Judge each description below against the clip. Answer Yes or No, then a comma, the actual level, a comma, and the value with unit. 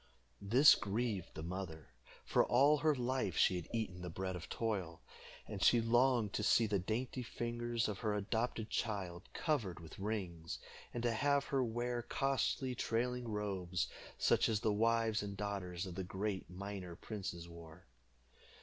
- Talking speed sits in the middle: Yes, average, 160 wpm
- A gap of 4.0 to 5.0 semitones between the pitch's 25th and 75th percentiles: Yes, average, 4.4 semitones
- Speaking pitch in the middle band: No, low, 105 Hz